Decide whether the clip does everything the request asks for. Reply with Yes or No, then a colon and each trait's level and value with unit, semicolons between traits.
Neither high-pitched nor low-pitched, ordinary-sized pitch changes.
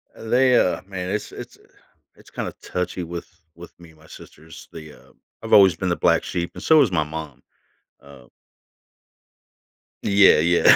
No: very low, 85 Hz; average, 3.4 semitones